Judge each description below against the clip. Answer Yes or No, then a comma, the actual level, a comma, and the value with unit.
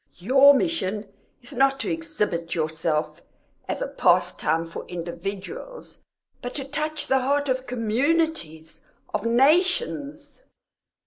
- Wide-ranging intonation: Yes, wide, 8.9 semitones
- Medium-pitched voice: No, very high, 260 Hz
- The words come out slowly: Yes, slow, 115 wpm